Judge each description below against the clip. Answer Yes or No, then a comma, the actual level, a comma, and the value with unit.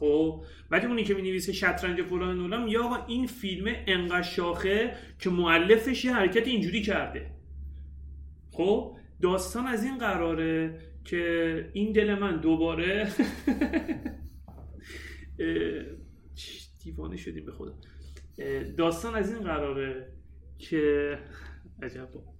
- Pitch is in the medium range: Yes, medium, 165 Hz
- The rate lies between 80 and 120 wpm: Yes, slow, 105 wpm